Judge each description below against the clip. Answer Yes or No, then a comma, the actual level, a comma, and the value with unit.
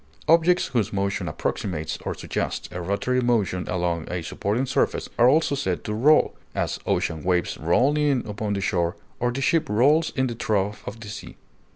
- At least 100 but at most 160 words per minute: No, average, 185 wpm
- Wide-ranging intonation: Yes, wide, 6.2 semitones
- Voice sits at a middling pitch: No, low, 110 Hz